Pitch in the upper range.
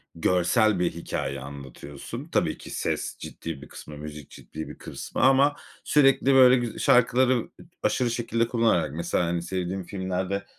No: very low, 95 Hz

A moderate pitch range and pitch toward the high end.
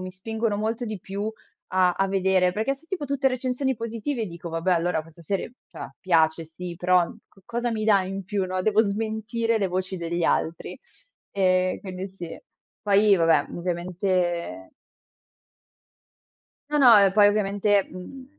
Yes: average, 3.4 semitones; high, 195 Hz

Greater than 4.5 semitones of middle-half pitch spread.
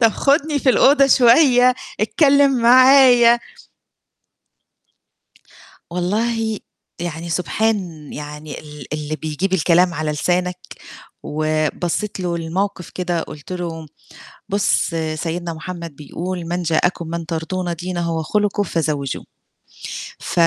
Yes: wide, 5.4 semitones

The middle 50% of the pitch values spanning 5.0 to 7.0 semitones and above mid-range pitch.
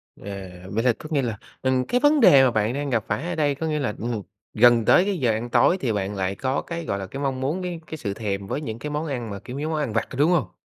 No: wide, 5.6 semitones; low, 130 Hz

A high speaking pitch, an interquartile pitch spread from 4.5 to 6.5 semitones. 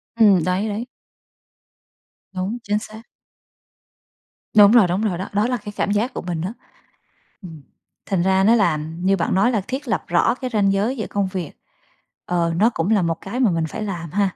No: high, 200 Hz; average, 3.4 semitones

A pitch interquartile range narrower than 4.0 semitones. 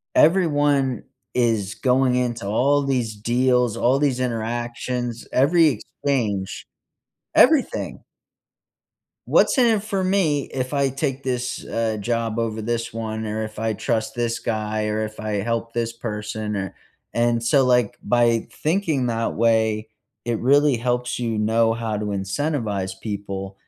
Yes: average, 3.1 semitones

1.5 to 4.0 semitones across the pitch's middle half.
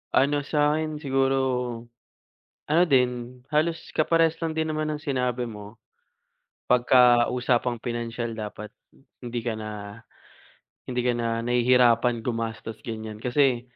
Yes: average, 3.7 semitones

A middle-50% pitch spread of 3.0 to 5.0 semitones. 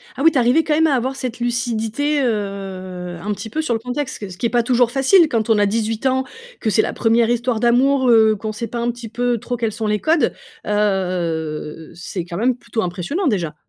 Yes: average, 3.6 semitones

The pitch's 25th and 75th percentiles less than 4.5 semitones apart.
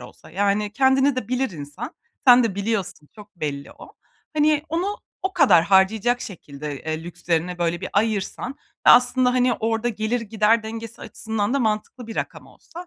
No: average, 5.0 semitones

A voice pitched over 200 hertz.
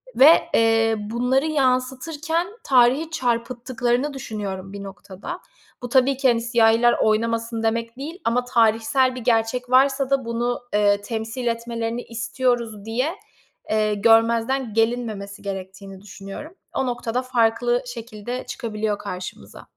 Yes: high, 235 Hz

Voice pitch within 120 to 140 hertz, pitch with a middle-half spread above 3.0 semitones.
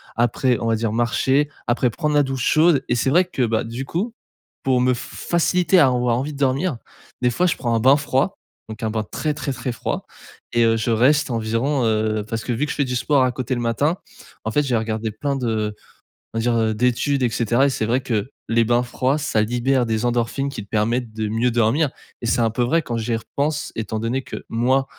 Yes: low, 125 Hz; average, 3.4 semitones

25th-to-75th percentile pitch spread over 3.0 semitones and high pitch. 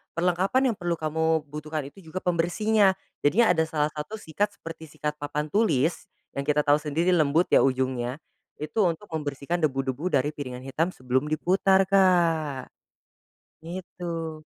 No: average, 3.5 semitones; medium, 160 Hz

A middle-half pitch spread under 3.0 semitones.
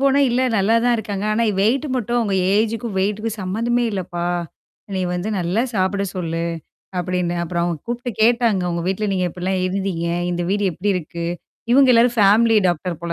No: average, 4.4 semitones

